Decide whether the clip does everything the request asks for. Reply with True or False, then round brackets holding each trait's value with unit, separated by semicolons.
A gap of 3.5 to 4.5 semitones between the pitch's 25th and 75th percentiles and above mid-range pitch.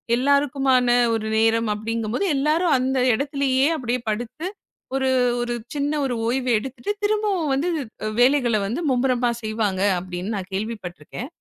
True (3.9 semitones; 250 Hz)